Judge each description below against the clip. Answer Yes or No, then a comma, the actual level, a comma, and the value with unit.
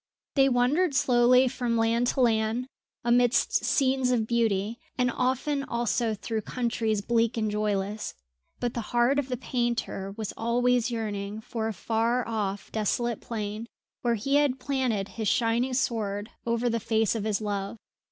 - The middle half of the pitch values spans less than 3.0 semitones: Yes, narrow, 2.4 semitones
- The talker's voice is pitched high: Yes, high, 235 Hz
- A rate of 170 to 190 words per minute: No, average, 155 wpm